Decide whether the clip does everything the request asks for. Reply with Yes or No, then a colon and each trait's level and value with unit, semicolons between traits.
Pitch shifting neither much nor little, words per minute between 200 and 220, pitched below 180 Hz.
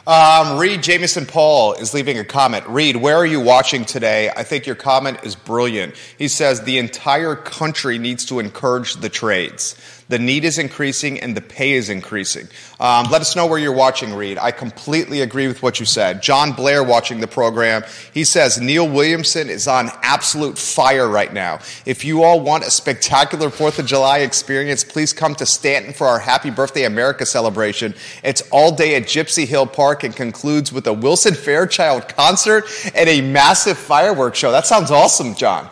No: average, 4.0 semitones; average, 190 wpm; low, 135 Hz